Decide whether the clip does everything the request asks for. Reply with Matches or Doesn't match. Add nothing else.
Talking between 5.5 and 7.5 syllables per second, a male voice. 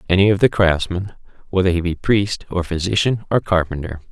Matches